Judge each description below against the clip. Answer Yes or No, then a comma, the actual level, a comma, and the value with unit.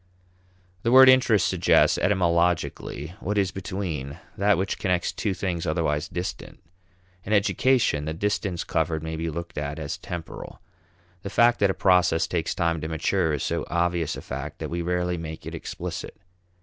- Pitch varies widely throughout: No, average, 3.2 semitones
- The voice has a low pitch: Yes, very low, 85 Hz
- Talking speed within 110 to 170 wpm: Yes, average, 165 wpm